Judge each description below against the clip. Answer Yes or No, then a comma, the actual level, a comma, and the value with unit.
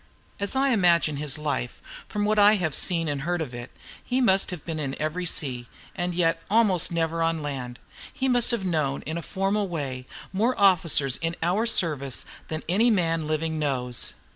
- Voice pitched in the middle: Yes, medium, 165 Hz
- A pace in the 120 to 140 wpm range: No, average, 190 wpm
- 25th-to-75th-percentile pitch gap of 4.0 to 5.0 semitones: Yes, average, 4.7 semitones